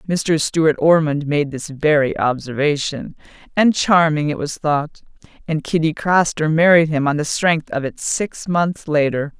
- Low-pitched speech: No, medium, 155 Hz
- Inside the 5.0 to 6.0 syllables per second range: No, 4.2 syllables/s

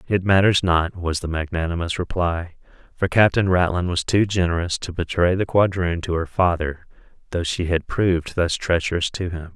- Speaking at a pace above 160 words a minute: Yes, average, 175 wpm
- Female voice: No, male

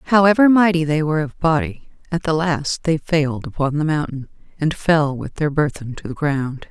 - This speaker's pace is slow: No, average, 195 wpm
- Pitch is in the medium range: Yes, medium, 155 Hz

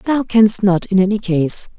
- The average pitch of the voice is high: Yes, high, 200 Hz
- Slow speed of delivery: No, average, 200 wpm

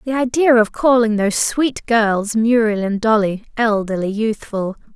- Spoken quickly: No, average, 145 wpm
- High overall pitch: Yes, high, 220 Hz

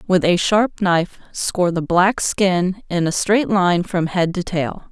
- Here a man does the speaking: No, female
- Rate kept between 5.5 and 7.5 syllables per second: No, 4.0 syllables/s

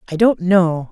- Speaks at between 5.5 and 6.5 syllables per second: No, 4.5 syllables/s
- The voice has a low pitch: No, medium, 185 Hz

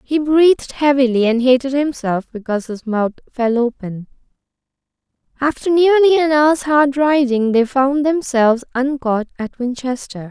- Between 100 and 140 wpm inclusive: Yes, slow, 135 wpm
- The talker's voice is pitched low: No, very high, 265 Hz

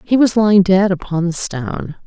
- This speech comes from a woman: Yes, female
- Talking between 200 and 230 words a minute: Yes, fast, 205 wpm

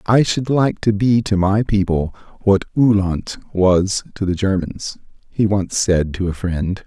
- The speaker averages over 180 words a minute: No, average, 175 wpm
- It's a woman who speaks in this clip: No, male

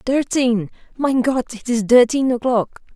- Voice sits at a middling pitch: No, high, 245 Hz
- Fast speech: No, slow, 120 wpm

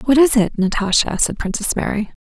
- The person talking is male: No, female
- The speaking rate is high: No, average, 190 wpm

